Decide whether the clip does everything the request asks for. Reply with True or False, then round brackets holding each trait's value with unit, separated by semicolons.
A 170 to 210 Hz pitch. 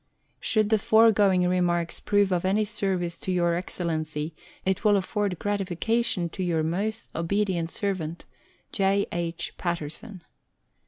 True (185 Hz)